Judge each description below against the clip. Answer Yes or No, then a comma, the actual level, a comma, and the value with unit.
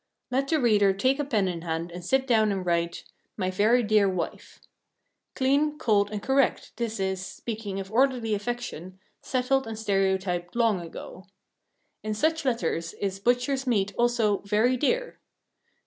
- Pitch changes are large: No, average, 4.7 semitones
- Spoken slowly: No, average, 155 wpm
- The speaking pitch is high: Yes, high, 215 Hz